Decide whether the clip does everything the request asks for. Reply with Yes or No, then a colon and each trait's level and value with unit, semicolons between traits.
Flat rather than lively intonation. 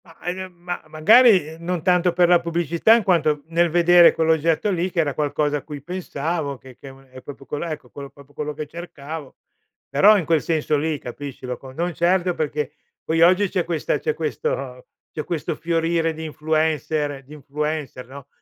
No: average, 3.0 semitones